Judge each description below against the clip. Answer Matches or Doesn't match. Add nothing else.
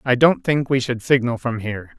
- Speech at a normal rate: Doesn't match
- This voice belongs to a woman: Doesn't match